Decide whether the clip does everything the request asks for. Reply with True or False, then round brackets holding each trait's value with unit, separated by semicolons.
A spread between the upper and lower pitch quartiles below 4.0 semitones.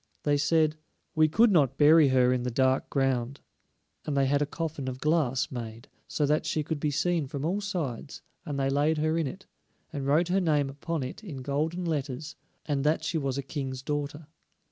True (2.8 semitones)